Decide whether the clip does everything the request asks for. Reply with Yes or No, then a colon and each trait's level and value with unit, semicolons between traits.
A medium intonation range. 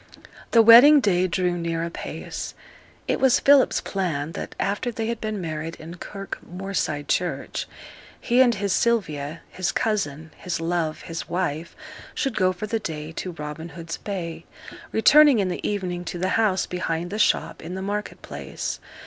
Yes: average, 4.4 semitones